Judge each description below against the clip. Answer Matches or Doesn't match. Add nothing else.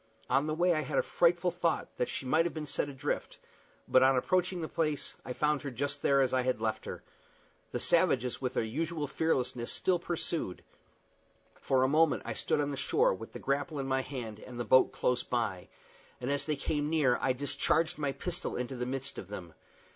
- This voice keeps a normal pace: Doesn't match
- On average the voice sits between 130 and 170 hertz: Matches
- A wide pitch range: Doesn't match